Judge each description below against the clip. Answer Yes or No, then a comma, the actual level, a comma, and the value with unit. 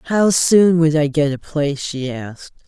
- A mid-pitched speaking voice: Yes, medium, 155 Hz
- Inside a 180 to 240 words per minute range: Yes, average, 200 wpm